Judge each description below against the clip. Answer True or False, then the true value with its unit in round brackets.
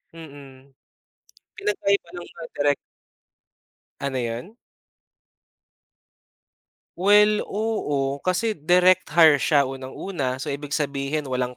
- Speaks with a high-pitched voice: False (145 Hz)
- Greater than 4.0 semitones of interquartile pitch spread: True (5.3 semitones)